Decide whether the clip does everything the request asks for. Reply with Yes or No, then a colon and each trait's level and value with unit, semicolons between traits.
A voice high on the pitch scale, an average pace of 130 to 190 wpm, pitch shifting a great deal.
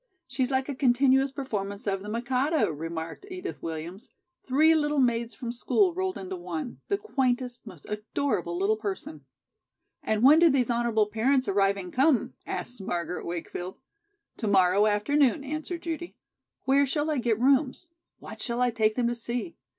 Yes: high, 240 Hz; average, 160 wpm; wide, 5.7 semitones